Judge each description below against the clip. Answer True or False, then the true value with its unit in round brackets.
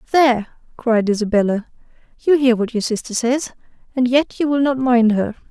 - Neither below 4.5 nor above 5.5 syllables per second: True (5.4 syllables/s)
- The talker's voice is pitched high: True (245 Hz)